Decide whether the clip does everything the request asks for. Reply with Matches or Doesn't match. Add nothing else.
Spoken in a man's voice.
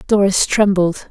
Doesn't match